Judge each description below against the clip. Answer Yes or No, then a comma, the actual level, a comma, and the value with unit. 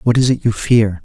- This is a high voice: No, low, 115 Hz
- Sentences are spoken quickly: Yes, fast, 290 wpm